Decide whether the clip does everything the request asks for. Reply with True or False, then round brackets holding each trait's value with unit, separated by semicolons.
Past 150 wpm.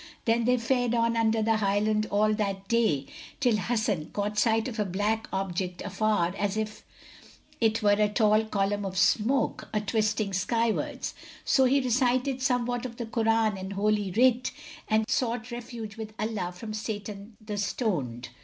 True (160 wpm)